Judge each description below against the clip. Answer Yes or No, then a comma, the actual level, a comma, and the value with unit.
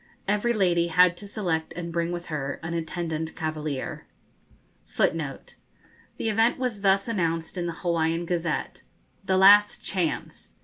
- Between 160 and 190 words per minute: No, average, 145 wpm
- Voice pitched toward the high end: No, medium, 170 Hz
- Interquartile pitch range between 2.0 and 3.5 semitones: Yes, average, 3.2 semitones